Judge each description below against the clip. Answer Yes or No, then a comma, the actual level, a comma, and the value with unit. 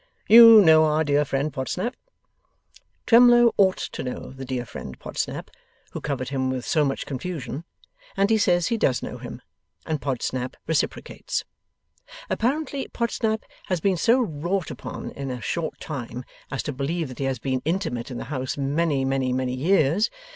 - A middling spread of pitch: No, wide, 6.5 semitones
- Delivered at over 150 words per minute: Yes, average, 170 wpm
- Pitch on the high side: No, medium, 150 Hz